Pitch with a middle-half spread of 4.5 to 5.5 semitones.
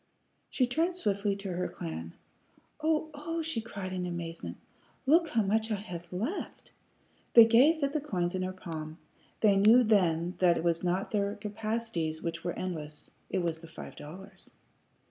Yes: average, 5.1 semitones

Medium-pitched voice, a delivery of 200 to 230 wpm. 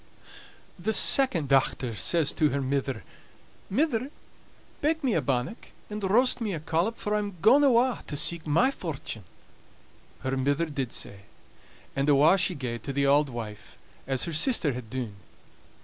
No: medium, 155 Hz; average, 165 wpm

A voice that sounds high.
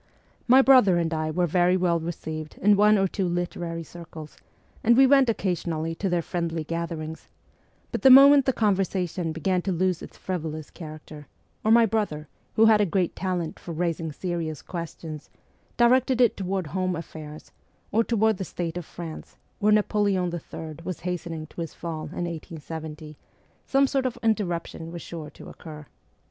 No: medium, 175 Hz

